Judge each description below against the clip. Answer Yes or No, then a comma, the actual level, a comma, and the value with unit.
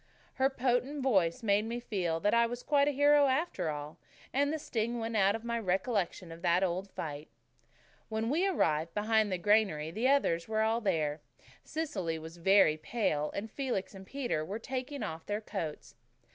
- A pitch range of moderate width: No, wide, 6.7 semitones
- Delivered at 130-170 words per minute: No, average, 185 wpm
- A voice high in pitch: Yes, high, 215 Hz